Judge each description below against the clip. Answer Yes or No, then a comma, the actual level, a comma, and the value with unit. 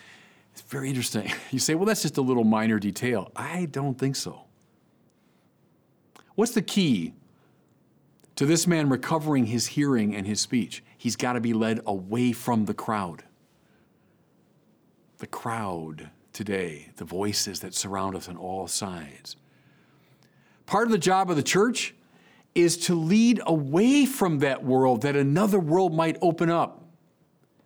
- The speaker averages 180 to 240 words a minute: No, average, 150 wpm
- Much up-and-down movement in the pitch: Yes, wide, 8.2 semitones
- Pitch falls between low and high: No, low, 130 Hz